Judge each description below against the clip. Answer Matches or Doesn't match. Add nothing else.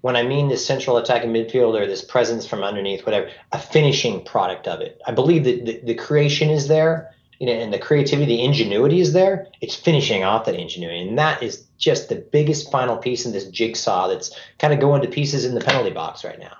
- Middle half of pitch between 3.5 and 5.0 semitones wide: Matches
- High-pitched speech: Doesn't match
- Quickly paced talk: Matches